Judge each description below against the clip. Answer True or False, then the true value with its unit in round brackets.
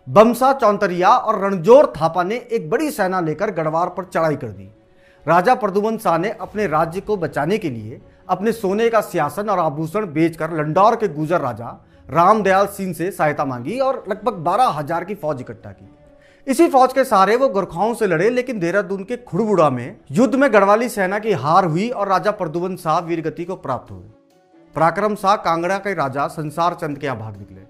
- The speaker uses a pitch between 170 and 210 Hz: True (185 Hz)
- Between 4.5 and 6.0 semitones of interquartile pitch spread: True (5.2 semitones)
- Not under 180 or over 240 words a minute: True (185 wpm)